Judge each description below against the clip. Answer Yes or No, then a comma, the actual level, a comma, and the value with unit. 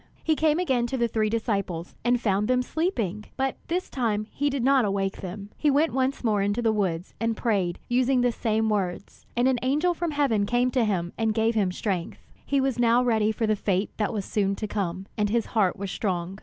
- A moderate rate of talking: No, fast, 225 wpm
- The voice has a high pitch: Yes, high, 225 Hz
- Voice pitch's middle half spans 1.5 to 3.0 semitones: No, average, 4.0 semitones